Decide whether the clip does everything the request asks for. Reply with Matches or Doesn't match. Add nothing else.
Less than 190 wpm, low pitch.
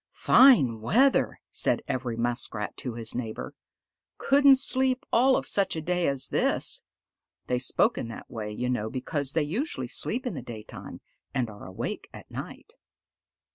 Matches